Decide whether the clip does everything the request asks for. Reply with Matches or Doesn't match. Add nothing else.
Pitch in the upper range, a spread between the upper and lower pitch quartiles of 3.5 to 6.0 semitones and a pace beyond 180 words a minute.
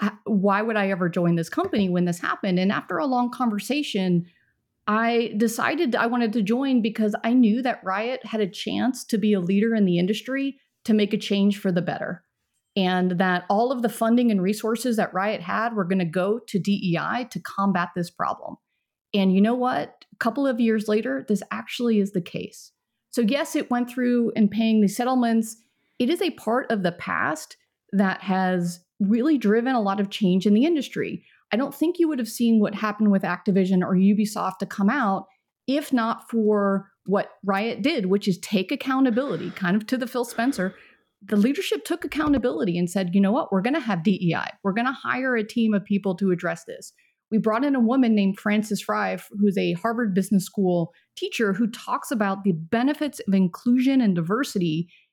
Matches